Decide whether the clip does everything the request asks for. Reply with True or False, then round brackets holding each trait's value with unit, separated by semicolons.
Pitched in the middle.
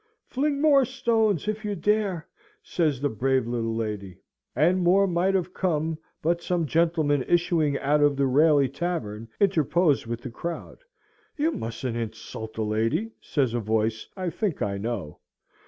True (155 Hz)